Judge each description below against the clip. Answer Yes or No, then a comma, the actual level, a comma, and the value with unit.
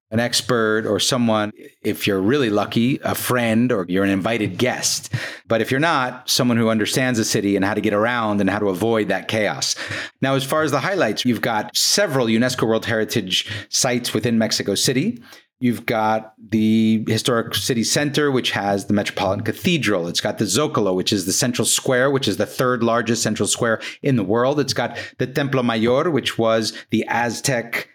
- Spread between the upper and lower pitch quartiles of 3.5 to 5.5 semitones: No, average, 3.0 semitones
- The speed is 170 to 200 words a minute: Yes, average, 195 wpm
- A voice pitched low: Yes, low, 115 Hz